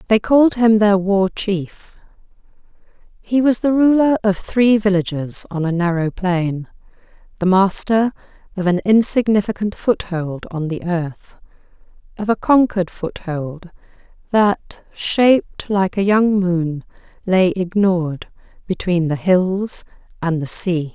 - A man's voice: No, female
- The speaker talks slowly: Yes, slow, 125 wpm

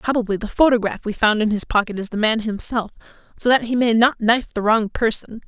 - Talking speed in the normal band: No, fast, 230 wpm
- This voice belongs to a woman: Yes, female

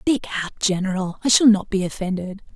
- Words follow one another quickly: No, average, 190 wpm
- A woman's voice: Yes, female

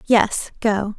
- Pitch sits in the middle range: No, high, 215 Hz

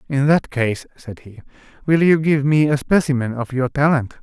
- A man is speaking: Yes, male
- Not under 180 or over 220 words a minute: Yes, average, 200 wpm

